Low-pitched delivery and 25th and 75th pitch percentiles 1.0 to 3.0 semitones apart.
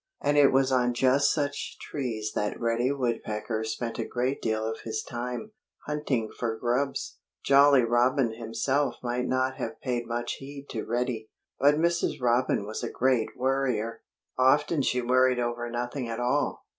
Yes: low, 125 Hz; average, 2.7 semitones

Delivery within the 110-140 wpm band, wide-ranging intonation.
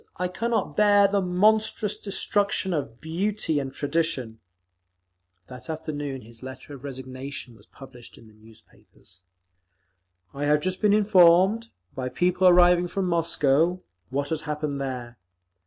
Yes: slow, 135 wpm; wide, 5.8 semitones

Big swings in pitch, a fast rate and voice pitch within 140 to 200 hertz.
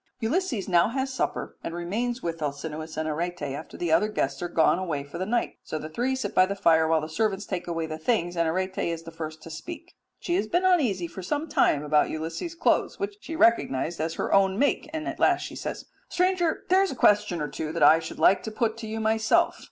Yes: wide, 7.1 semitones; fast, 240 wpm; medium, 185 Hz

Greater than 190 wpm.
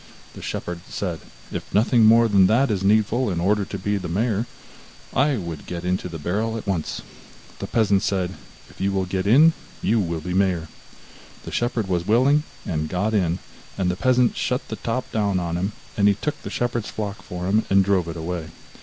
Yes: average, 200 wpm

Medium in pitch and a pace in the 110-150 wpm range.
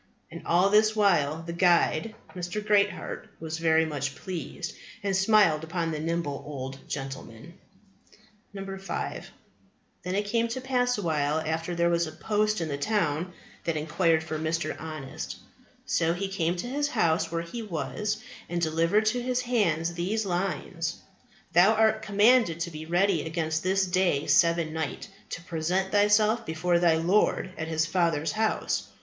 No: medium, 170 Hz; average, 160 wpm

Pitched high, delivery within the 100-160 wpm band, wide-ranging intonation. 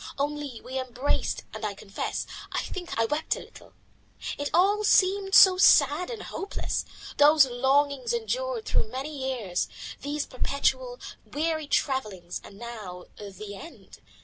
Yes: very high, 285 Hz; average, 140 wpm; wide, 7.1 semitones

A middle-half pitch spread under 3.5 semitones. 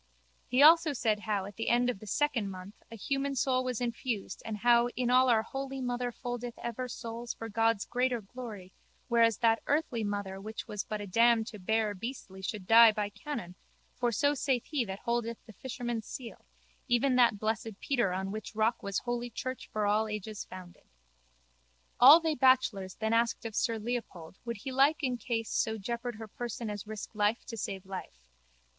Yes: average, 2.9 semitones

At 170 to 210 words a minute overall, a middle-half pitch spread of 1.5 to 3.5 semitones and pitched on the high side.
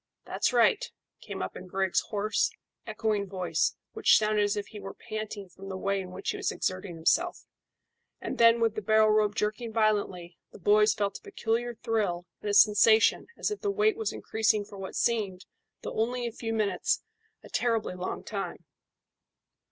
Yes: average, 185 wpm; narrow, 2.6 semitones; high, 215 Hz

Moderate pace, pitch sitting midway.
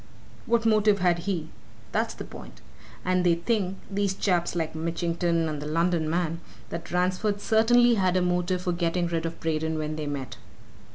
Yes: average, 175 wpm; medium, 175 Hz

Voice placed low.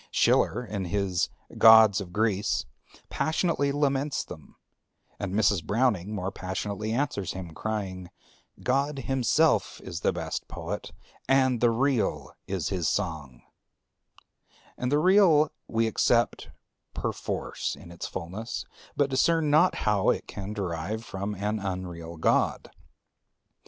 Yes: low, 105 Hz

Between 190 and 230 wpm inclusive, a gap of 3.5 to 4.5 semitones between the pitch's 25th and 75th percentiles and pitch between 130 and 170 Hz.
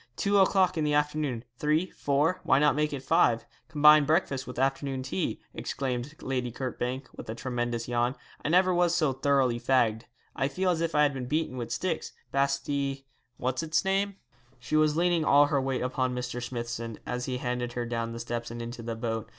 Yes: average, 200 wpm; average, 3.8 semitones; low, 135 Hz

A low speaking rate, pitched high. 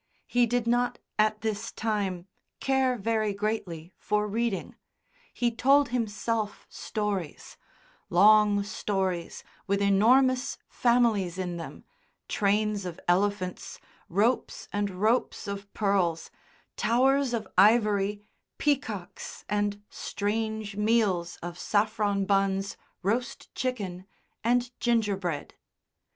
Yes: slow, 100 wpm; high, 210 Hz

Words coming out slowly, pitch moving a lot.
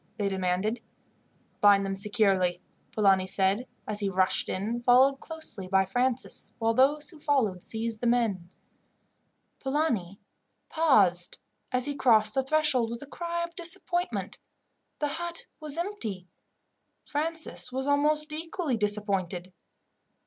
Yes: slow, 125 wpm; wide, 7.3 semitones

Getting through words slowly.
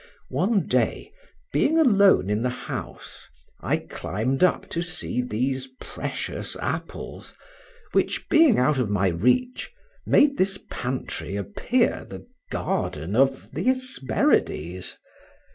Yes: slow, 110 wpm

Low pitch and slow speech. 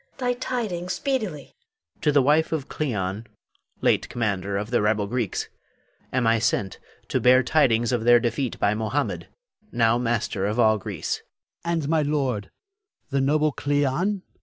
No: low, 125 Hz; average, 160 wpm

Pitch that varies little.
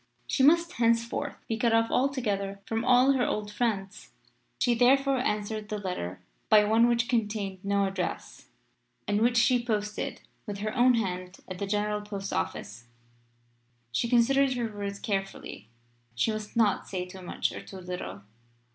No: average, 3.4 semitones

